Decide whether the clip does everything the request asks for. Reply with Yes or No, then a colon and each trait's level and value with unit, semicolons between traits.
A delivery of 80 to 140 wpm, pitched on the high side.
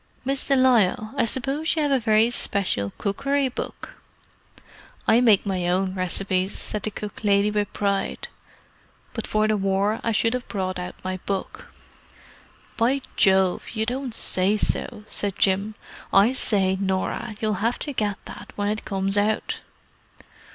No: average, 160 wpm; high, 210 Hz